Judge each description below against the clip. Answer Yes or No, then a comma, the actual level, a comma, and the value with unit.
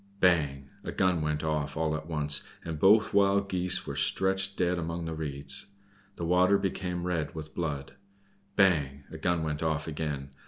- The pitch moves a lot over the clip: No, average, 3.4 semitones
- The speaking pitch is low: Yes, very low, 80 Hz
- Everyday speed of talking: Yes, average, 170 wpm